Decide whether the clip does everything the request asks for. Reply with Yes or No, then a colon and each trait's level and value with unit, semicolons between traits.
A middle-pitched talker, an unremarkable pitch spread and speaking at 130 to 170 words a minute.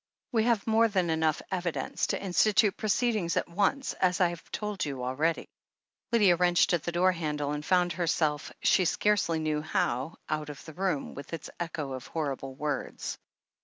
No: medium, 170 Hz; average, 4.3 semitones; average, 185 wpm